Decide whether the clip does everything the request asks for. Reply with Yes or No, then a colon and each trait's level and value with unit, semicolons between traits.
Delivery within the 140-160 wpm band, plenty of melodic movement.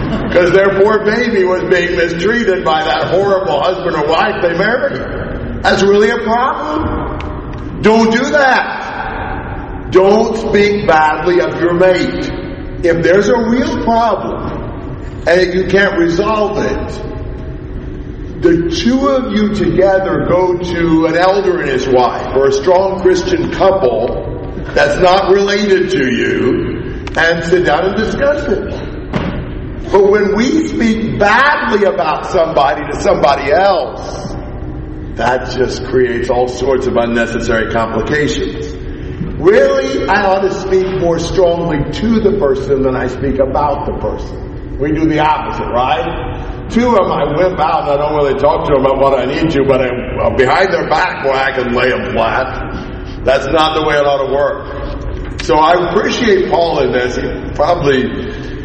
Yes: average, 155 wpm; wide, 6.3 semitones